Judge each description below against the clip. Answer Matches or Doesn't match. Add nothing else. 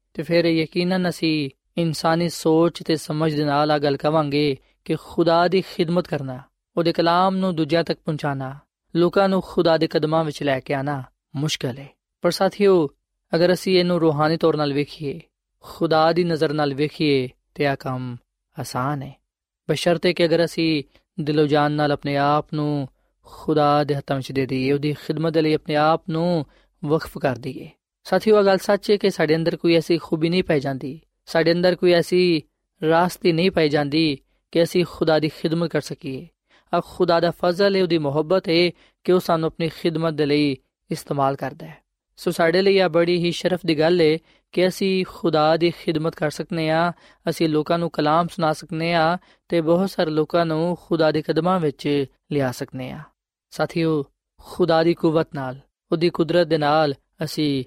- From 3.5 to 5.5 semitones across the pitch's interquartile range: Doesn't match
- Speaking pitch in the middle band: Matches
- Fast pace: Matches